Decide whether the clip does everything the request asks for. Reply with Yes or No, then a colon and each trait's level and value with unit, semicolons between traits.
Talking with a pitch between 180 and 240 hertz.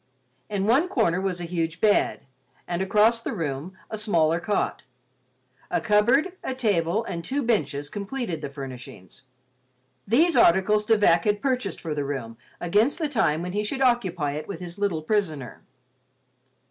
Yes: high, 190 Hz